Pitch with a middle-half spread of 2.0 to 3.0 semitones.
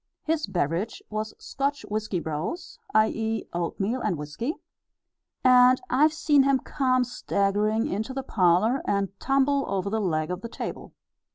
No: wide, 5.4 semitones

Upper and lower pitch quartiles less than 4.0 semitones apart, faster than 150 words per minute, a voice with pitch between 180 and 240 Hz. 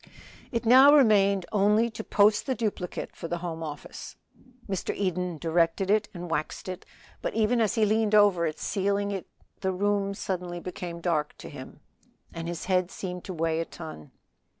Yes: average, 3.4 semitones; average, 175 wpm; high, 190 Hz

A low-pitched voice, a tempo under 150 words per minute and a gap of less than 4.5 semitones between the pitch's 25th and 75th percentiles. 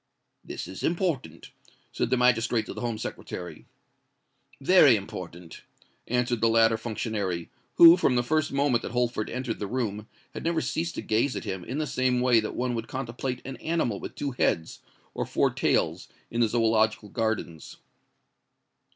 No: low, 120 Hz; average, 170 wpm; average, 3.1 semitones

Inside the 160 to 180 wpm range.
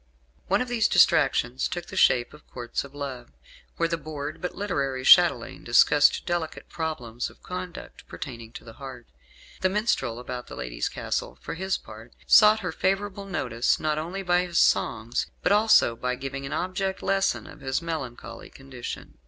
Yes: average, 170 wpm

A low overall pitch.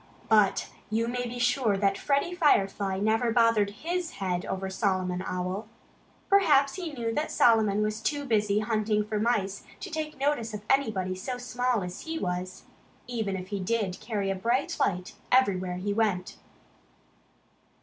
No: high, 215 Hz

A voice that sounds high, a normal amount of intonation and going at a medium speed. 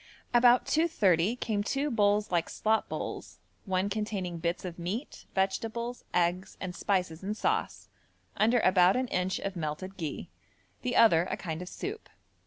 Yes: high, 195 Hz; average, 4.3 semitones; average, 155 wpm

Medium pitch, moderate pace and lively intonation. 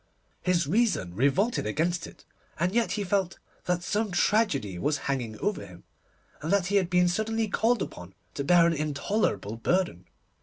Yes: medium, 175 Hz; average, 165 wpm; wide, 6.6 semitones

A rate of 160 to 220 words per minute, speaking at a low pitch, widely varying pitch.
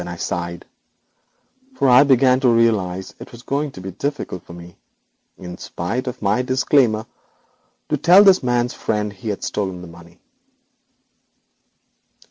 No: average, 150 wpm; low, 115 Hz; wide, 6.2 semitones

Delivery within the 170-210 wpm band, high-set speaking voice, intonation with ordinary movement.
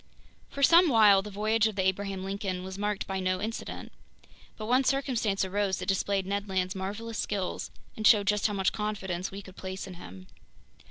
No: average, 195 wpm; high, 200 Hz; narrow, 2.1 semitones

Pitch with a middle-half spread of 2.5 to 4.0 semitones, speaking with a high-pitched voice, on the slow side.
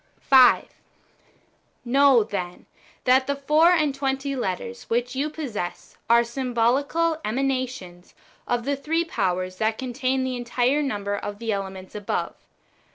No: average, 4.5 semitones; very high, 250 Hz; slow, 130 wpm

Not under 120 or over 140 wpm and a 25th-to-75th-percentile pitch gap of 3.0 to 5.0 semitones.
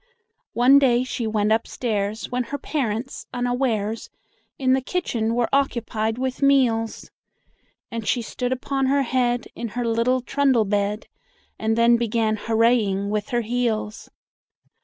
No: slow, 135 wpm; narrow, 2.6 semitones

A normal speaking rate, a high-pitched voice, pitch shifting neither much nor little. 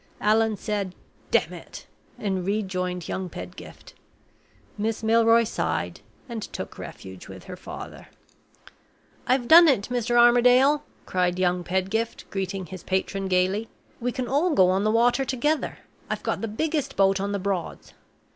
Yes: average, 145 wpm; high, 210 Hz; average, 4.2 semitones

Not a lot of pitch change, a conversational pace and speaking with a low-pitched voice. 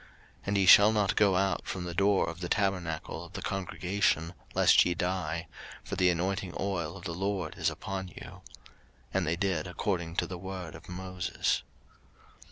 Yes: narrow, 2.1 semitones; average, 180 wpm; very low, 90 Hz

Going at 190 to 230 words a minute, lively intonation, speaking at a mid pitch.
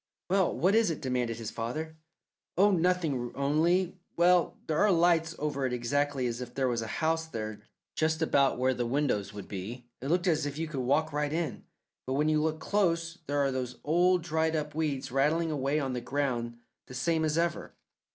No: average, 200 wpm; average, 4.5 semitones; medium, 150 Hz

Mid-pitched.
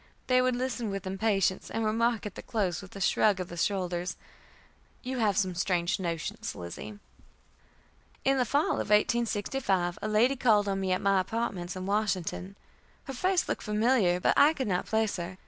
No: high, 205 Hz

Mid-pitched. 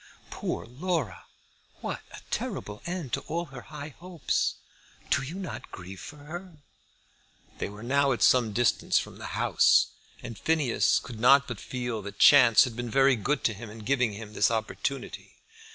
No: low, 125 Hz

